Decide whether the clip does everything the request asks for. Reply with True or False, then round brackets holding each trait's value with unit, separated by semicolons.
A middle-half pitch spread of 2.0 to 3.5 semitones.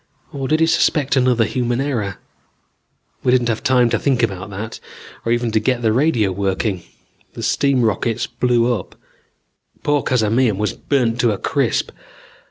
True (3.1 semitones)